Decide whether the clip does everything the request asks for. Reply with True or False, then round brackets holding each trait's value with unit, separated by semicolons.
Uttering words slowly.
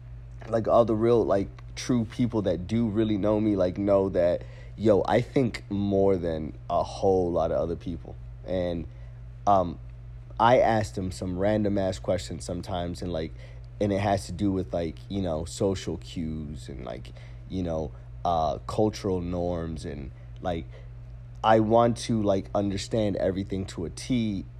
False (165 wpm)